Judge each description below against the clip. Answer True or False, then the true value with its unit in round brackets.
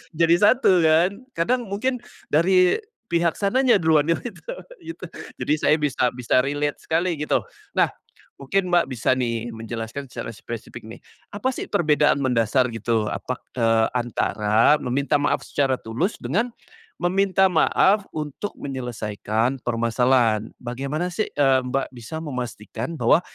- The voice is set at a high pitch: False (140 Hz)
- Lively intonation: True (6.6 semitones)